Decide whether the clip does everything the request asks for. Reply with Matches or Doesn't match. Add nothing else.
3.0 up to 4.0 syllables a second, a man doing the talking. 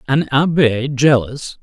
Matches